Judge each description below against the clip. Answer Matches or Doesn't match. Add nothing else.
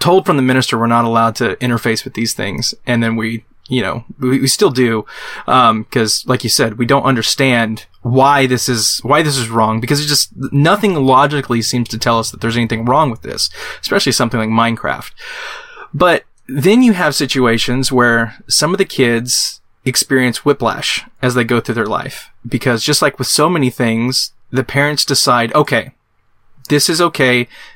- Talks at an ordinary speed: Matches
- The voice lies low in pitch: Matches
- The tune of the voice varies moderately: Matches